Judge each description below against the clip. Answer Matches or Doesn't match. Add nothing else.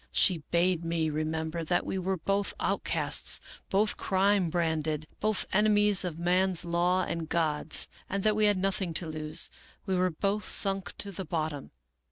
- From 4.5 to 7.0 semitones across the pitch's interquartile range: Doesn't match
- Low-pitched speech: Doesn't match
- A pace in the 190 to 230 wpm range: Doesn't match